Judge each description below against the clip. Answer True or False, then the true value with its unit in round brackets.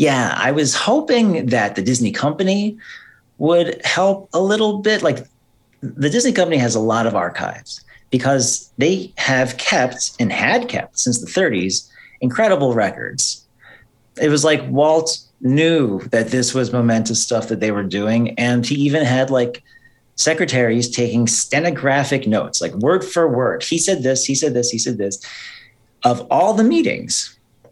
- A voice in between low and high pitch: False (130 Hz)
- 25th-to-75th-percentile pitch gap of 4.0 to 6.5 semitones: True (5.2 semitones)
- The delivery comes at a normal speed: True (160 wpm)